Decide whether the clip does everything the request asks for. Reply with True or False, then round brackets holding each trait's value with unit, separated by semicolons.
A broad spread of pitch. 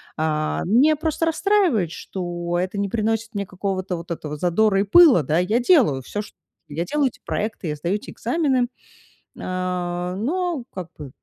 True (6.0 semitones)